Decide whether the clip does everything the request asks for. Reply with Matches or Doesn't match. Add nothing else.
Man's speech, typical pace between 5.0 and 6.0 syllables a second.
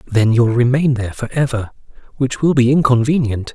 Matches